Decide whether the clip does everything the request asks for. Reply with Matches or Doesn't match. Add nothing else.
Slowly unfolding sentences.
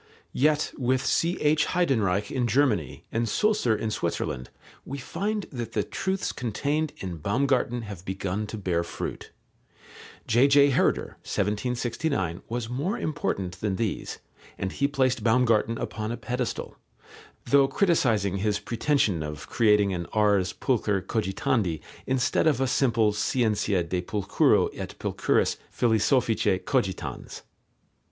Matches